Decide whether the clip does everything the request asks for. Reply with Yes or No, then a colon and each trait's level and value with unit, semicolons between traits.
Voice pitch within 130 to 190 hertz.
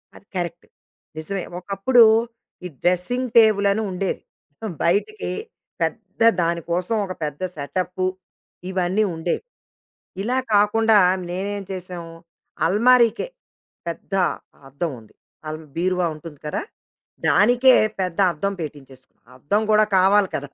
Yes: medium, 185 Hz